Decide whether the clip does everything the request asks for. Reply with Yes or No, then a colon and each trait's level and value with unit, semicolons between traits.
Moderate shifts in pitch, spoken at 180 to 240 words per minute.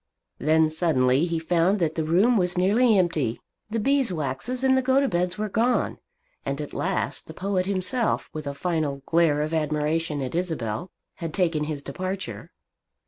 No: average, 4.5 semitones; average, 160 wpm